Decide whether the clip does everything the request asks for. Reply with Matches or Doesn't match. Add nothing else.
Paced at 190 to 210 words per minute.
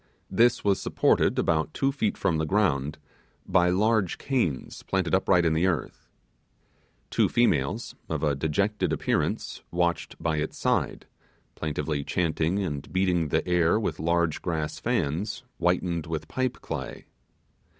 Doesn't match